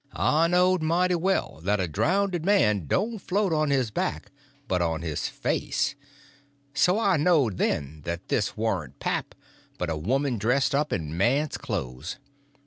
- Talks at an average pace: Yes, average, 160 wpm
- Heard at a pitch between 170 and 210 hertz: No, low, 135 Hz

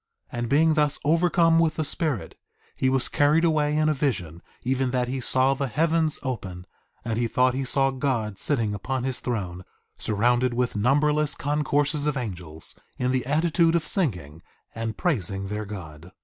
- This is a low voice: Yes, low, 130 Hz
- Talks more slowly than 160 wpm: No, average, 175 wpm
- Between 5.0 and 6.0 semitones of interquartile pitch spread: Yes, wide, 5.4 semitones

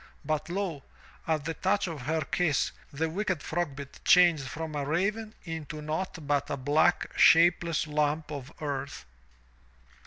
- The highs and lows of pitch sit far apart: No, average, 3.0 semitones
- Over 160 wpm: No, average, 145 wpm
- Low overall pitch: No, medium, 155 Hz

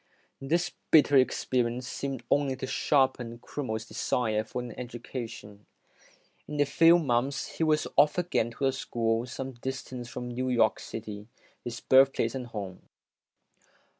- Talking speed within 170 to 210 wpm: No, average, 140 wpm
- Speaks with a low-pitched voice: Yes, low, 125 Hz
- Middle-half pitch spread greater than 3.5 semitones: No, average, 2.7 semitones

